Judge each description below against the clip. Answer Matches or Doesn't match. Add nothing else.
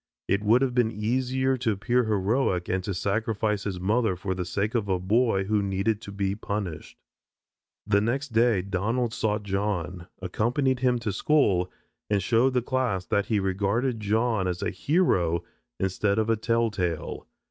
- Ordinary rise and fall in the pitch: Matches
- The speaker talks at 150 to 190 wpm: Matches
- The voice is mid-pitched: Doesn't match